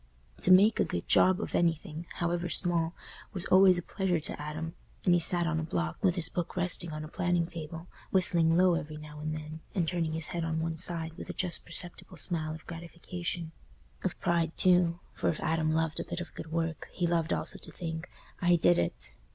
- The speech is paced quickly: Yes, fast, 210 wpm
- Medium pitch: Yes, medium, 165 Hz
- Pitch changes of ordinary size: No, narrow, 1.7 semitones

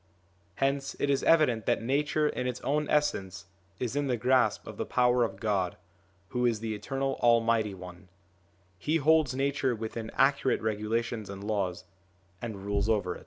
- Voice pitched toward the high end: No, low, 115 Hz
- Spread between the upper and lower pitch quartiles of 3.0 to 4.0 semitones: No, average, 4.6 semitones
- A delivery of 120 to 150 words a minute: No, average, 170 wpm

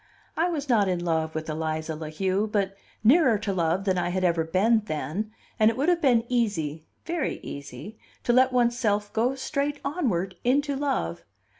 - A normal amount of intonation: No, wide, 7.1 semitones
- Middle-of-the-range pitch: No, high, 210 Hz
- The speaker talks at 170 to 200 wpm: Yes, average, 185 wpm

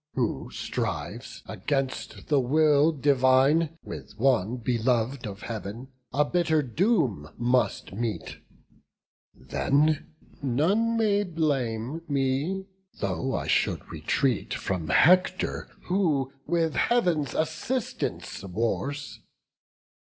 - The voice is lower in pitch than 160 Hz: Yes, medium, 140 Hz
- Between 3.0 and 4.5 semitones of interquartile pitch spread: No, average, 5.2 semitones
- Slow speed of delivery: Yes, slow, 95 wpm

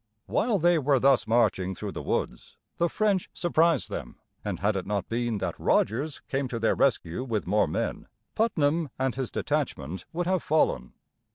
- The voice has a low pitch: Yes, low, 130 Hz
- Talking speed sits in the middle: Yes, average, 175 wpm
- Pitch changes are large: Yes, wide, 7.4 semitones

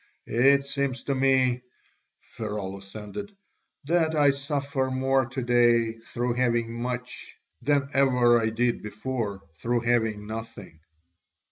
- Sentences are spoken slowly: Yes, slow, 120 wpm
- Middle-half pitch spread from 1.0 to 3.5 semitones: Yes, average, 3.0 semitones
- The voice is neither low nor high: No, low, 120 Hz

